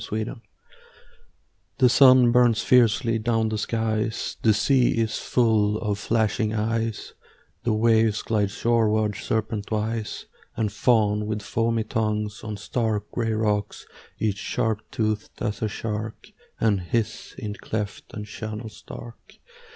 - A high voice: No, low, 110 Hz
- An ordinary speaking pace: No, slow, 130 wpm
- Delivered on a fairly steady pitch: Yes, narrow, 1.4 semitones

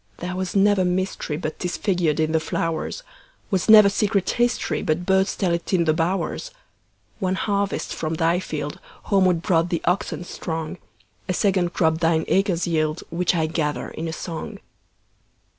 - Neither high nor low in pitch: Yes, medium, 175 Hz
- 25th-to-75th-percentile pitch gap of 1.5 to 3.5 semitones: Yes, average, 3.0 semitones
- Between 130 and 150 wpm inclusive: Yes, average, 140 wpm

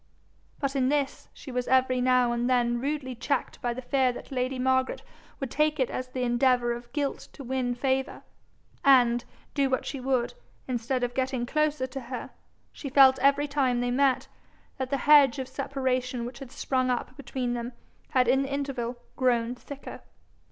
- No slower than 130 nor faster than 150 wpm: No, average, 180 wpm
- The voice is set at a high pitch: Yes, very high, 255 Hz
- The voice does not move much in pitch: Yes, narrow, 1.8 semitones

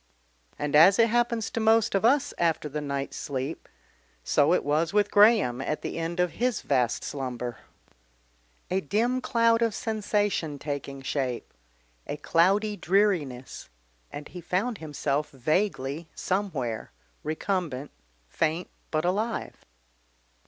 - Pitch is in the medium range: Yes, medium, 170 Hz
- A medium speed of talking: No, slow, 130 wpm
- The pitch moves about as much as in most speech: No, wide, 6.6 semitones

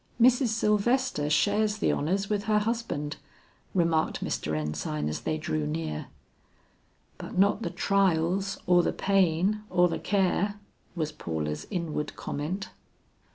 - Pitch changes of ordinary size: No, wide, 5.7 semitones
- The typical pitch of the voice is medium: Yes, medium, 180 Hz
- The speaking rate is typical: No, slow, 130 wpm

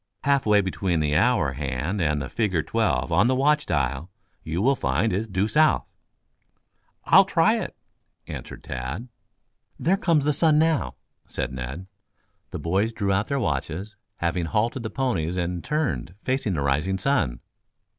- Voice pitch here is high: No, very low, 95 Hz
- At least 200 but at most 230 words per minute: No, average, 160 wpm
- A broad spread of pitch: Yes, wide, 8.5 semitones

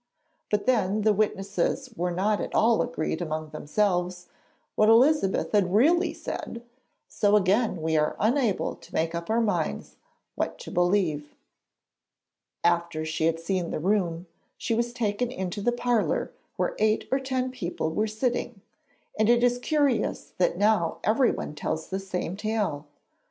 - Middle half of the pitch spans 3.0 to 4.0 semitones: No, average, 5.3 semitones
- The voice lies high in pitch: Yes, high, 205 Hz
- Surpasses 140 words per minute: Yes, average, 150 wpm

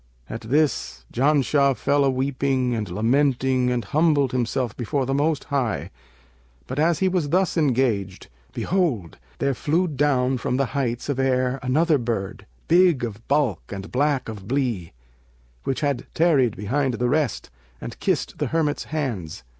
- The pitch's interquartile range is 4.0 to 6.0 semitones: No, average, 3.6 semitones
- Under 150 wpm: No, average, 155 wpm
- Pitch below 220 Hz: Yes, low, 135 Hz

